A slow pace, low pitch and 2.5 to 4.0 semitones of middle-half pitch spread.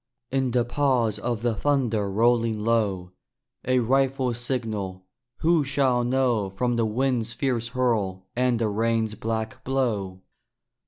Yes: slow, 130 wpm; low, 120 Hz; average, 2.9 semitones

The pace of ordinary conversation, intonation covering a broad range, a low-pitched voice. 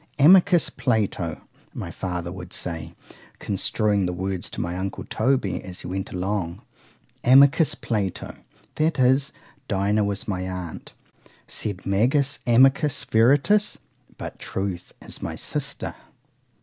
No: slow, 115 wpm; wide, 6.3 semitones; low, 100 Hz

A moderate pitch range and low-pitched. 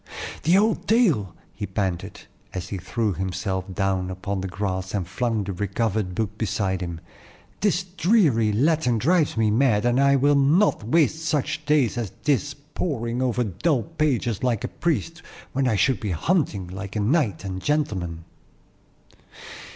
No: wide, 7.2 semitones; low, 115 Hz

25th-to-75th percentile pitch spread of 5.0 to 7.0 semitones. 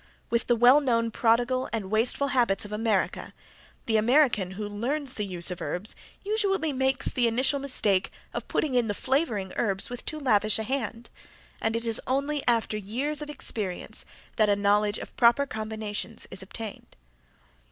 No: average, 4.1 semitones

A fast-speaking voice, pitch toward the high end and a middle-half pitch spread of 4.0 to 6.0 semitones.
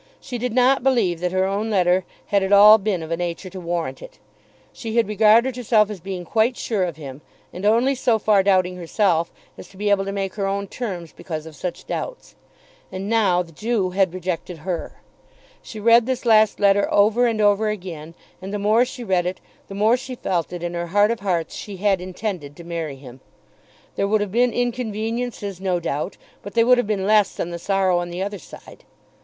No: fast, 215 wpm; high, 200 Hz; average, 3.6 semitones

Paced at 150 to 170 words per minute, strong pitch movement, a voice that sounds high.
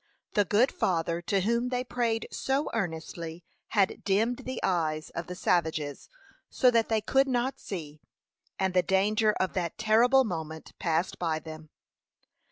Yes: average, 155 wpm; wide, 6.0 semitones; high, 195 Hz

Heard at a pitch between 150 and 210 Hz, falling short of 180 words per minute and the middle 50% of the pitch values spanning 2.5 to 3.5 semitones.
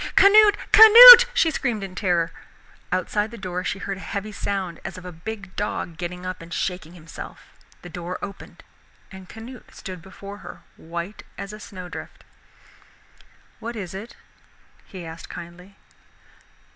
Yes: high, 190 Hz; average, 155 wpm; average, 3.2 semitones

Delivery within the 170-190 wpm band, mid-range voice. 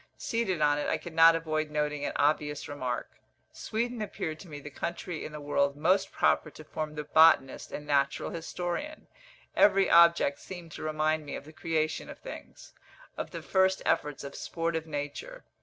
Yes: average, 180 wpm; medium, 155 Hz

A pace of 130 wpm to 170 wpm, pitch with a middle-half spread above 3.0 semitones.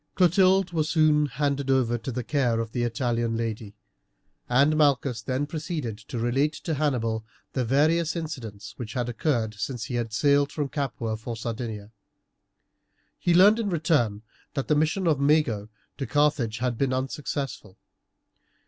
Yes: average, 155 wpm; average, 4.8 semitones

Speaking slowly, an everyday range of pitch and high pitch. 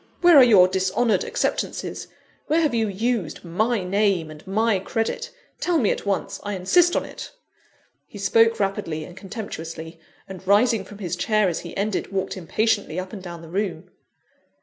No: average, 170 wpm; average, 3.6 semitones; high, 200 Hz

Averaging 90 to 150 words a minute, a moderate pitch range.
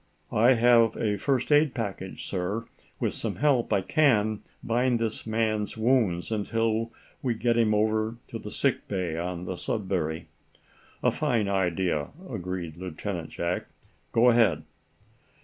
Yes: average, 140 wpm; average, 4.2 semitones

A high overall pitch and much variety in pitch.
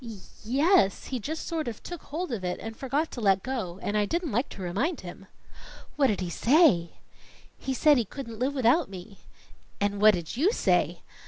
Yes: high, 235 Hz; wide, 6.6 semitones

